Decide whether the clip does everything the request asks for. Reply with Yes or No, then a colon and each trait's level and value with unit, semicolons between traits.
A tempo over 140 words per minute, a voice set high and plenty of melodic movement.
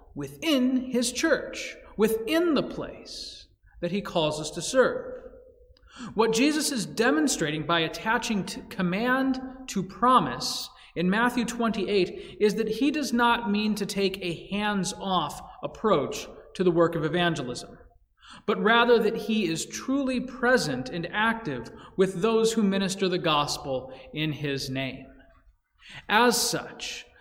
No: slow, 135 wpm; high, 210 Hz; wide, 6.2 semitones